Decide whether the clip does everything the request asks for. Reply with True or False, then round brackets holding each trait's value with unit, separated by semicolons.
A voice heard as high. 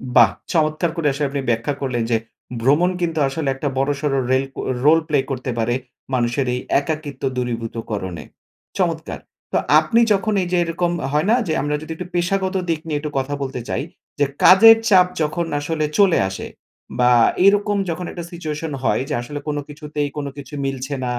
False (150 Hz)